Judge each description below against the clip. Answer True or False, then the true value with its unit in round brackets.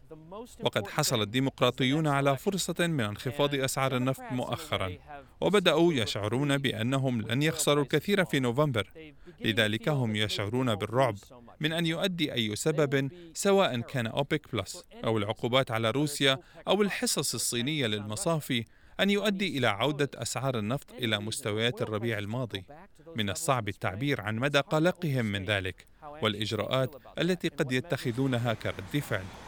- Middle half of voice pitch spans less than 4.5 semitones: False (5.3 semitones)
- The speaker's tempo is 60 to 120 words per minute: False (130 wpm)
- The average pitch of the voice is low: True (130 Hz)